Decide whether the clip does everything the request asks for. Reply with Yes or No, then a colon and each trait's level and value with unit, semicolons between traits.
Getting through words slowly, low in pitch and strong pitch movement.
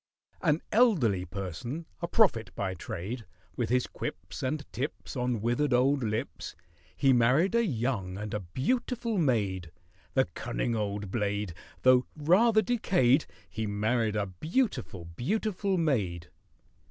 Yes: slow, 130 wpm; low, 125 Hz; wide, 7.4 semitones